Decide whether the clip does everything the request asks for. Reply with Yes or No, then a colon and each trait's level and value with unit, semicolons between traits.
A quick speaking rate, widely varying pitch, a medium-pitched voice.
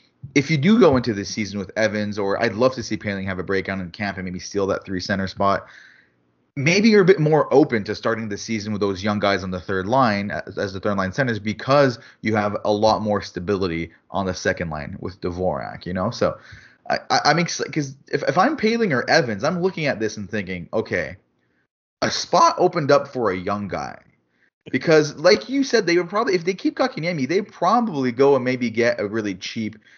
No: fast, 225 wpm; wide, 7.0 semitones; low, 110 Hz